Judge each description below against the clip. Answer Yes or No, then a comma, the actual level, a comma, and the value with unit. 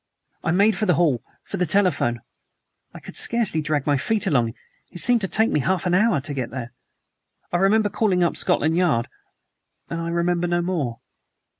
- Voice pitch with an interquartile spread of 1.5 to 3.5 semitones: No, average, 5.0 semitones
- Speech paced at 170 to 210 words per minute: Yes, average, 190 wpm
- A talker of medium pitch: Yes, medium, 175 Hz